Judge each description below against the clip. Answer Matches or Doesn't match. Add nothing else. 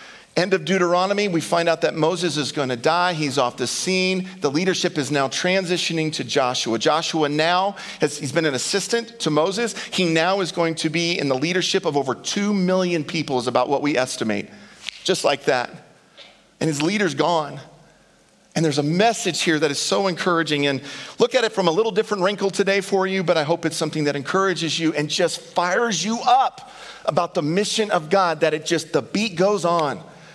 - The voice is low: Doesn't match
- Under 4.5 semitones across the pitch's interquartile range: Matches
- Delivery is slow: Doesn't match